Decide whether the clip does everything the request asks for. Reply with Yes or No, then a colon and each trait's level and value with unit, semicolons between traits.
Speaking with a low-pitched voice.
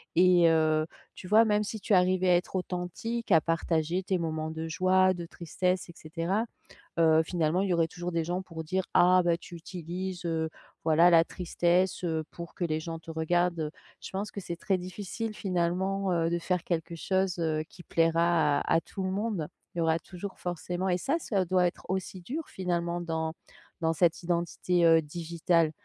No: medium, 175 Hz